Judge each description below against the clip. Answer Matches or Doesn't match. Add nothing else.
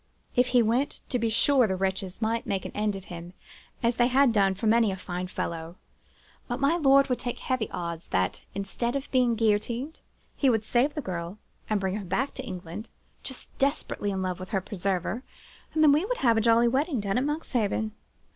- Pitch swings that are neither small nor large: Matches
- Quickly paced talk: Matches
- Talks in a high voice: Matches